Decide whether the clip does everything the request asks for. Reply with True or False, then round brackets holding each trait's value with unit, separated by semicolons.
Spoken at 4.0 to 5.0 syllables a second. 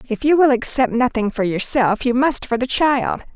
True (4.9 syllables/s)